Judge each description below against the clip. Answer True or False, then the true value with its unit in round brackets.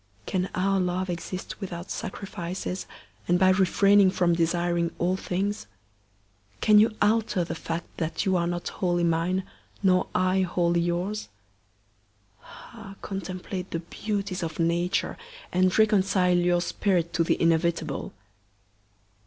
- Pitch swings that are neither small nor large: False (2.0 semitones)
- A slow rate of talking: True (130 wpm)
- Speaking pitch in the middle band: True (180 Hz)